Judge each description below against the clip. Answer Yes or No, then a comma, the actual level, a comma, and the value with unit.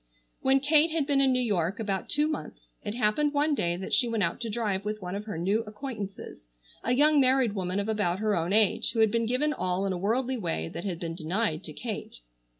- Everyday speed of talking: No, fast, 240 wpm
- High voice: Yes, high, 215 Hz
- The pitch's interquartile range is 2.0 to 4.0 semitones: No, wide, 5.6 semitones